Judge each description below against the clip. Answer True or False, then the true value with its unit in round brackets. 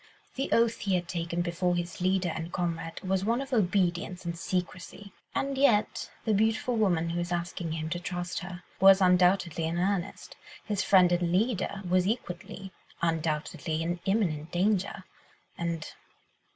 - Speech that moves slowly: False (155 wpm)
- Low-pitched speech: False (180 Hz)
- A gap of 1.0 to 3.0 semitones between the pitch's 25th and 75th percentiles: True (2.6 semitones)